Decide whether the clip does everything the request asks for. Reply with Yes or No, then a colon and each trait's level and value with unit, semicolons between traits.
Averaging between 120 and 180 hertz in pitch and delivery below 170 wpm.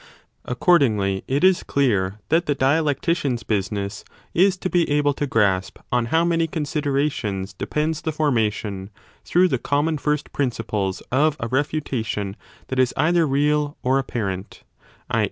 Yes: medium, 140 Hz; average, 150 wpm